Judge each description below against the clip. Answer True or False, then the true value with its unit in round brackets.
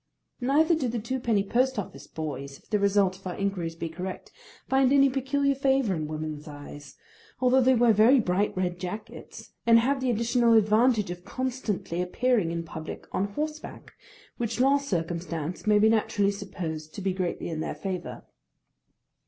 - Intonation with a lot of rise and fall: True (6.2 semitones)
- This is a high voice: True (210 Hz)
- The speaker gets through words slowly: False (170 wpm)